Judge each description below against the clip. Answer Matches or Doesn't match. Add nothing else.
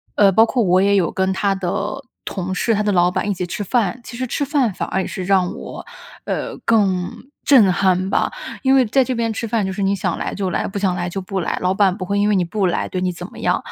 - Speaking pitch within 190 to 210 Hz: Matches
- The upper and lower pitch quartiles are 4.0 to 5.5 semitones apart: Doesn't match